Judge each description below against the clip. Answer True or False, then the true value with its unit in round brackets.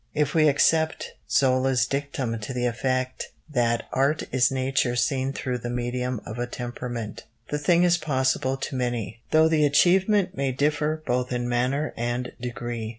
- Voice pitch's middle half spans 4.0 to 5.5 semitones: False (3.2 semitones)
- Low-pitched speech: True (130 Hz)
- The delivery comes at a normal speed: True (160 wpm)